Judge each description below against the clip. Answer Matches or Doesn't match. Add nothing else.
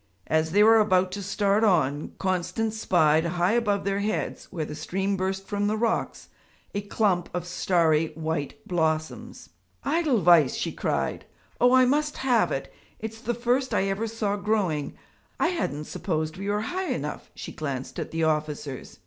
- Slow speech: Doesn't match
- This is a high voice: Matches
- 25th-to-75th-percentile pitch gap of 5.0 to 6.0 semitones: Matches